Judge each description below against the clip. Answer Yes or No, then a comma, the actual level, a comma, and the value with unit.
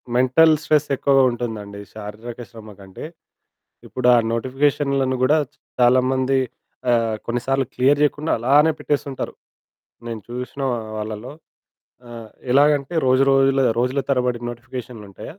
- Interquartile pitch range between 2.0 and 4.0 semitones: Yes, narrow, 2.6 semitones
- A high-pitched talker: No, low, 130 Hz